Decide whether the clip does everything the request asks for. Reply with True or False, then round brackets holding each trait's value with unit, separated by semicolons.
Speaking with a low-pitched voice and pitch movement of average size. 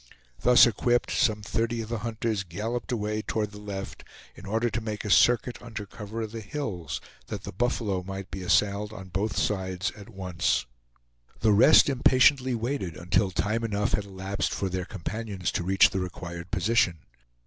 True (105 Hz; 3.3 semitones)